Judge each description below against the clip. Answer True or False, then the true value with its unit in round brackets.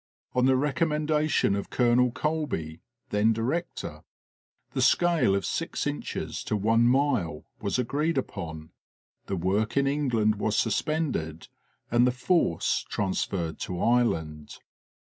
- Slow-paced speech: True (125 wpm)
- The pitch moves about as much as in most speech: False (6.6 semitones)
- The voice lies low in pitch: True (120 Hz)